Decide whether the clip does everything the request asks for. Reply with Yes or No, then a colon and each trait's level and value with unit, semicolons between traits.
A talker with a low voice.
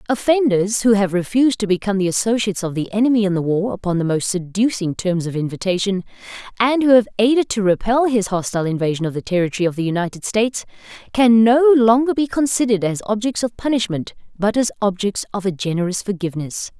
No: high, 205 Hz